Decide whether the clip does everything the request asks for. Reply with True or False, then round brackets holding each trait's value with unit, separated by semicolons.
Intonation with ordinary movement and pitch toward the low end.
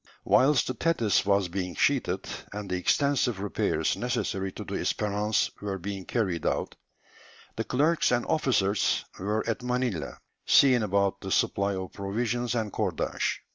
True (3.9 semitones; 105 Hz)